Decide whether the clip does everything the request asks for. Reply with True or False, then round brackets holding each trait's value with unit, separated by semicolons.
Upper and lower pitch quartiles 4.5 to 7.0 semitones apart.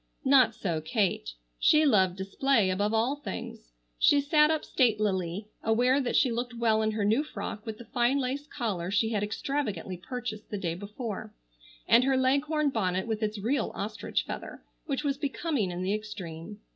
True (4.9 semitones)